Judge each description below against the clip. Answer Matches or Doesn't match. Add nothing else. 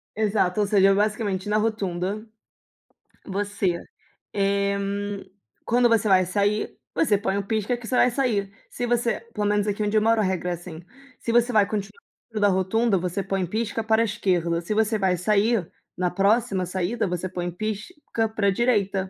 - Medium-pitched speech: Doesn't match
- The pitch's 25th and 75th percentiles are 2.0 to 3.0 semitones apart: Matches